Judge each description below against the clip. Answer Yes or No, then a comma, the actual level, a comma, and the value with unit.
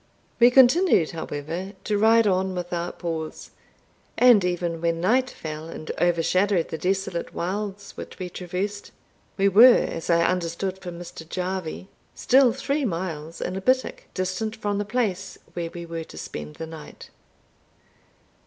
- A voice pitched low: No, medium, 185 Hz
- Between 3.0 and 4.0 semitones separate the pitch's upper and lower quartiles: Yes, average, 3.5 semitones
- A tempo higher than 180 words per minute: No, average, 150 wpm